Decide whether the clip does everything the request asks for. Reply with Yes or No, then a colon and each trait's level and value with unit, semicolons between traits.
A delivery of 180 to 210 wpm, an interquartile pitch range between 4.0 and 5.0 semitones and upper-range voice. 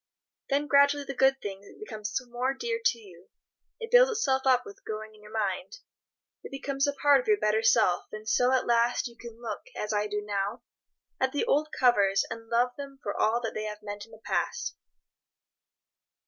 Yes: average, 195 wpm; average, 4.5 semitones; high, 240 Hz